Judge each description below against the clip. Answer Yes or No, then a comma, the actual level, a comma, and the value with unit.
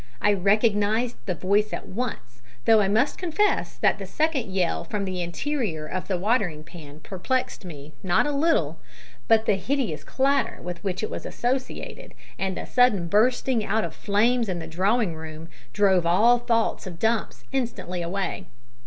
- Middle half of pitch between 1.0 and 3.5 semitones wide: No, wide, 5.4 semitones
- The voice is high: Yes, high, 205 Hz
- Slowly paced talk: No, average, 170 wpm